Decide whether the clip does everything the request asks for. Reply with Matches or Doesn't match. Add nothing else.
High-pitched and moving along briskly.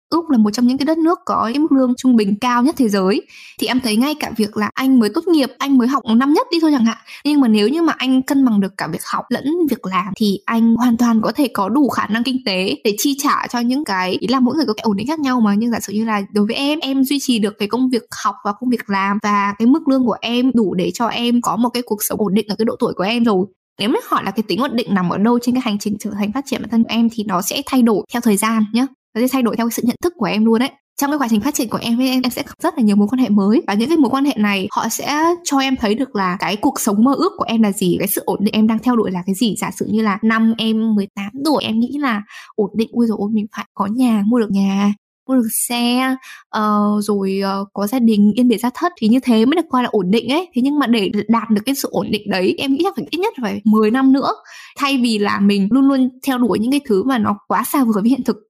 Matches